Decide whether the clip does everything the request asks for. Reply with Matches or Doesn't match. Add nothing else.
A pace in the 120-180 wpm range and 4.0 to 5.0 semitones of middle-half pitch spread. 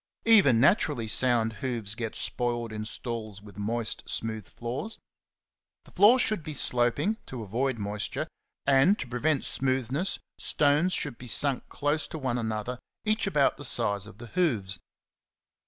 Matches